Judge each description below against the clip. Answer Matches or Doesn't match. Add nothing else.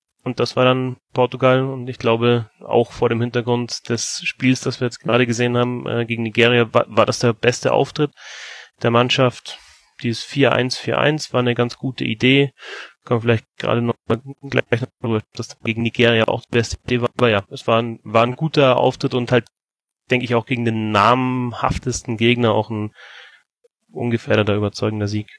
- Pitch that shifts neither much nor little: Doesn't match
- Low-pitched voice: Matches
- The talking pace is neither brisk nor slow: Matches